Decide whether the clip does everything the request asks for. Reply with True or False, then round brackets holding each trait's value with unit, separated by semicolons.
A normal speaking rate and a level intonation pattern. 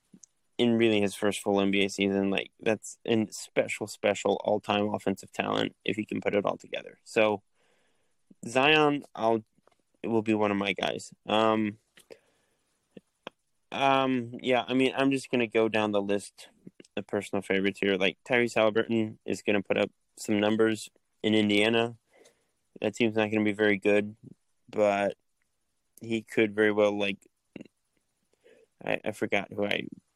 True (155 wpm; 2.2 semitones)